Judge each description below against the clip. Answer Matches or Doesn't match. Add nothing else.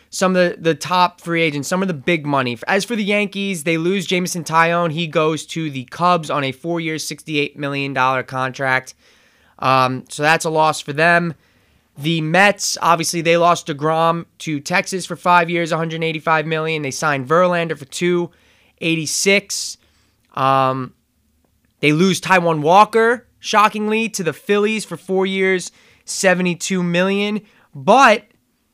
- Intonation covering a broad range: Doesn't match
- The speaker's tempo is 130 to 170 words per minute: Matches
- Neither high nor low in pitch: Matches